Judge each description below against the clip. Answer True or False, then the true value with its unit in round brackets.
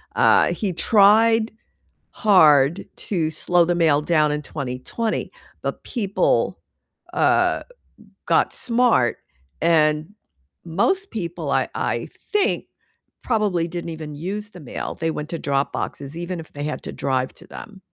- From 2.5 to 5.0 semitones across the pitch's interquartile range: False (5.5 semitones)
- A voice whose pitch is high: False (170 Hz)